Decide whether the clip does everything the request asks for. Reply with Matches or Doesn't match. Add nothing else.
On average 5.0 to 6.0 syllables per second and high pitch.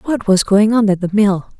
Matches